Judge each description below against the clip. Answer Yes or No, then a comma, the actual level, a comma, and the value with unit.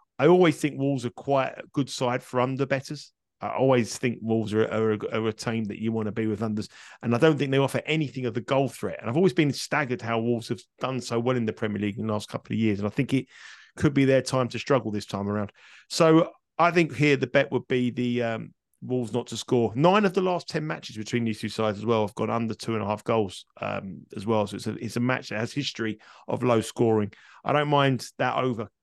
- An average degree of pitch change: Yes, average, 3.7 semitones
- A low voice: Yes, low, 120 Hz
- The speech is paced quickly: Yes, fast, 265 wpm